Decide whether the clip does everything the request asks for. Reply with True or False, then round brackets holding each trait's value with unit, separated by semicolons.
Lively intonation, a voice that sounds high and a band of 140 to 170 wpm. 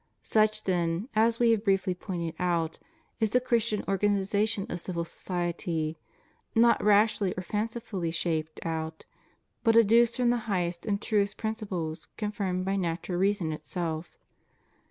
False (4.2 semitones; 195 Hz; 145 wpm)